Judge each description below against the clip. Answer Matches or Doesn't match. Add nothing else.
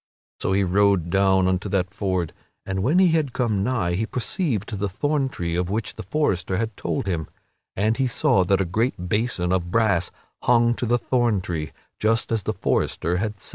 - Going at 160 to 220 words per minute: Matches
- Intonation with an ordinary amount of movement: Matches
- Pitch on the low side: Matches